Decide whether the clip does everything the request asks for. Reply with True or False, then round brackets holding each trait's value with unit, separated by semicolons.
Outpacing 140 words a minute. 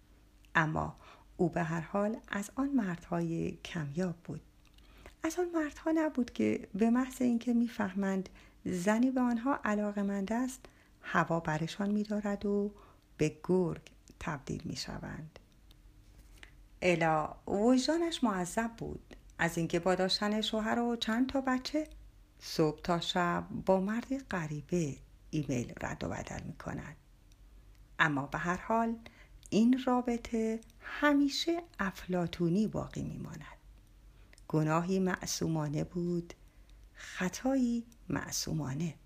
False (115 wpm)